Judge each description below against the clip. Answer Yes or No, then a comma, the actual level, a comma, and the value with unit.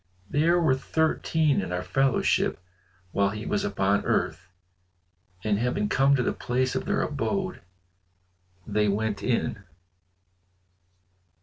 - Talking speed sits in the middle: No, slow, 120 wpm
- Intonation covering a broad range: Yes, wide, 6.7 semitones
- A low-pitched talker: Yes, low, 125 Hz